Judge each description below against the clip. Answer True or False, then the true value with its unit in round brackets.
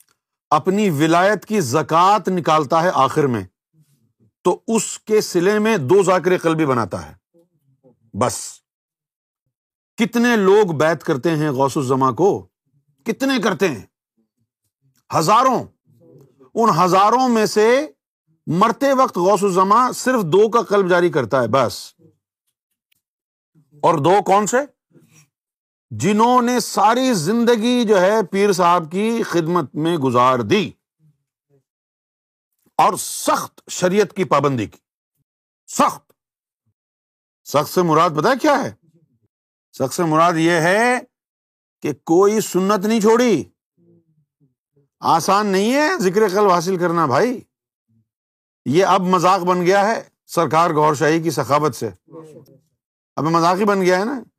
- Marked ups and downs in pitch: True (6.5 semitones)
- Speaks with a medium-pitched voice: True (170 Hz)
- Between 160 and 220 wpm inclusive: False (125 wpm)